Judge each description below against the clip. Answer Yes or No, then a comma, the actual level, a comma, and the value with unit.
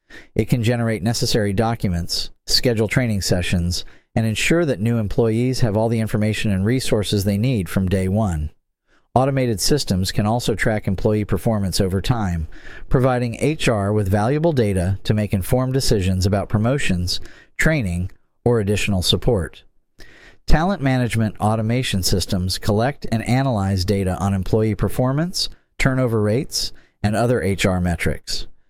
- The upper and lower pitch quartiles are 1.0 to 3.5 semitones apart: No, average, 4.1 semitones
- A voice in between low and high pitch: No, low, 105 Hz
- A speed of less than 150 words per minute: Yes, slow, 135 wpm